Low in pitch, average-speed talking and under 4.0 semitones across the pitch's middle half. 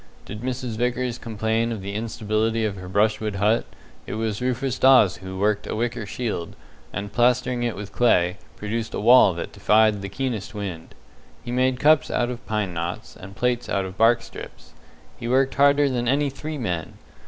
Yes: low, 115 Hz; average, 185 wpm; average, 3.5 semitones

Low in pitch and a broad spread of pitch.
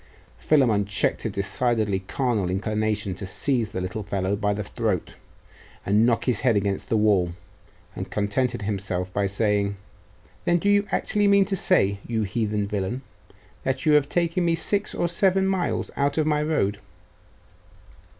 Yes: low, 110 Hz; wide, 6.8 semitones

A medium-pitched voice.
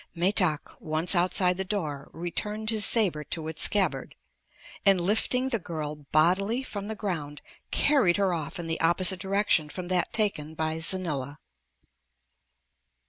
Yes: medium, 180 Hz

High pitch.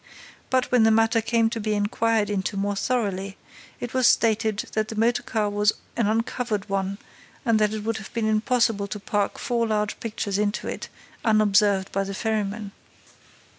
Yes: high, 215 Hz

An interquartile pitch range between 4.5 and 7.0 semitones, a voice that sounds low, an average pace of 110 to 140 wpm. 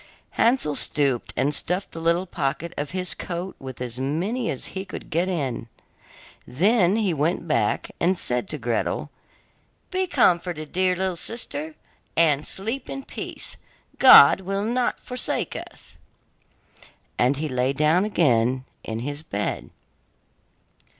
No: wide, 5.5 semitones; medium, 165 Hz; slow, 135 wpm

